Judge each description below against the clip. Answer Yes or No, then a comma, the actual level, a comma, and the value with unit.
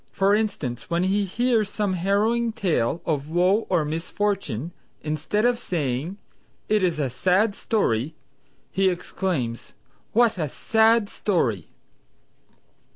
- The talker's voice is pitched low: No, medium, 185 Hz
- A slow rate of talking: Yes, slow, 120 wpm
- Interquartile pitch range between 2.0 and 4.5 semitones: No, wide, 5.5 semitones